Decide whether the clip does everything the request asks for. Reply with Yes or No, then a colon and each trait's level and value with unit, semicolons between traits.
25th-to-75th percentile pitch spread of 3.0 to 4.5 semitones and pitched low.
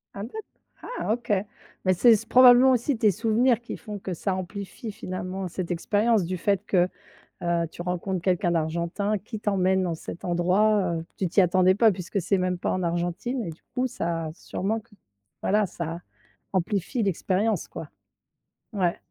No: average, 3.5 semitones; high, 190 Hz